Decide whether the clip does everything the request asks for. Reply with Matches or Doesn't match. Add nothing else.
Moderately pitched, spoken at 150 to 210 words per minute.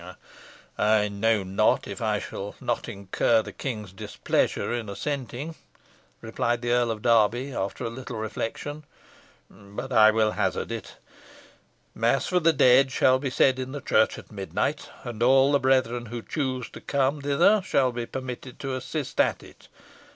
Doesn't match